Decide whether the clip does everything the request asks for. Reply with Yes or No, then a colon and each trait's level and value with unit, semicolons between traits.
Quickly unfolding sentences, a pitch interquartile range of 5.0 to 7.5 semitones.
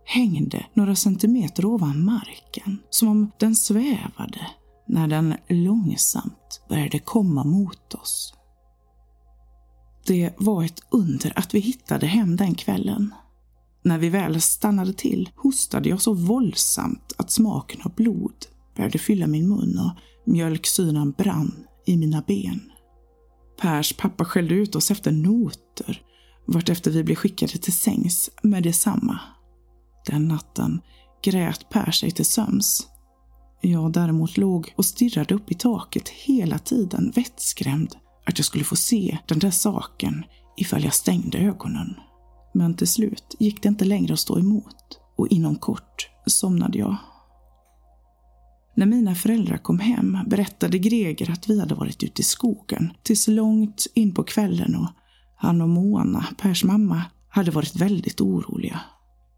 No: average, 140 wpm; wide, 5.5 semitones